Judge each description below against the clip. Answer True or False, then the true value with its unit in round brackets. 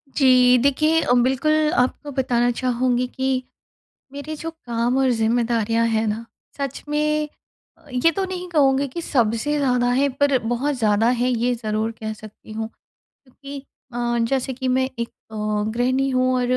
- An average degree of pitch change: True (3.0 semitones)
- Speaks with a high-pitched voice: True (255 Hz)